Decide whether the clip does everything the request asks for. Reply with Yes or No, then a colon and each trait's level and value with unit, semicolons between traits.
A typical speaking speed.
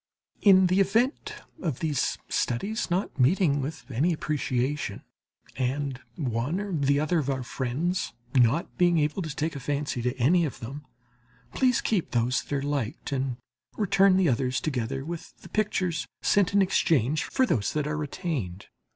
Yes: average, 165 wpm